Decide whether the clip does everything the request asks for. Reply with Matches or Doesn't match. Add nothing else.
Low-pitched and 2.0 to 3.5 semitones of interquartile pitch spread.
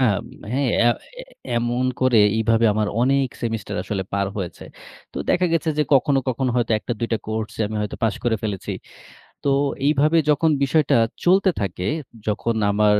Doesn't match